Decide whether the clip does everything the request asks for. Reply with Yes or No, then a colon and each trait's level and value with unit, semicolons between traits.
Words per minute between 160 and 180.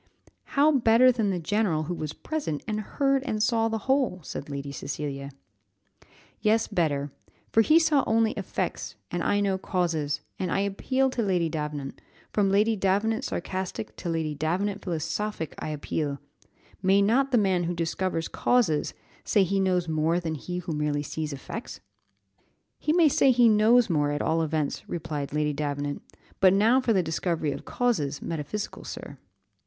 Yes: average, 165 wpm